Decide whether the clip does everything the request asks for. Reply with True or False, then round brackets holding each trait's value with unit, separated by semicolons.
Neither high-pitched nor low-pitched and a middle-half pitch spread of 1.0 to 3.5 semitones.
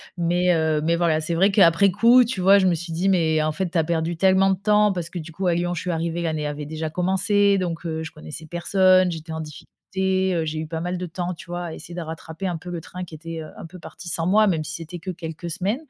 True (175 Hz; 2.5 semitones)